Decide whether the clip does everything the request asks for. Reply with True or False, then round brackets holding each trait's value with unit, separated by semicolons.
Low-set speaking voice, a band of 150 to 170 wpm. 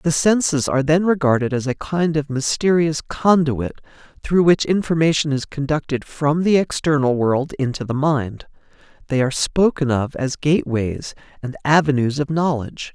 False (145 Hz; 155 wpm)